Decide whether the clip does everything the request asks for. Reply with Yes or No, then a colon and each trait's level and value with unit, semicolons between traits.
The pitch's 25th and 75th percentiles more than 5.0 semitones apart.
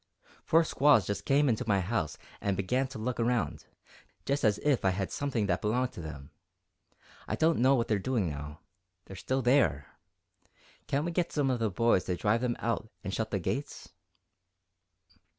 Yes: wide, 5.5 semitones